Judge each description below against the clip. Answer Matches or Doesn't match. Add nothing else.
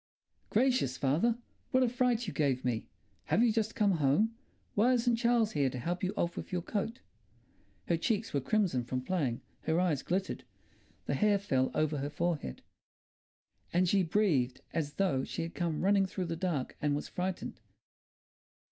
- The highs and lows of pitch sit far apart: Matches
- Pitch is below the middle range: Doesn't match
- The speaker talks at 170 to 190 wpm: Matches